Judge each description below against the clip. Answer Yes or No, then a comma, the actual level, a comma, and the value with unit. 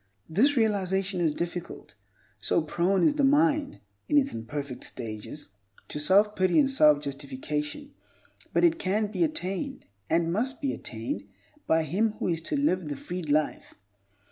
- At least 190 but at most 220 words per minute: No, average, 155 wpm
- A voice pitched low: No, medium, 185 Hz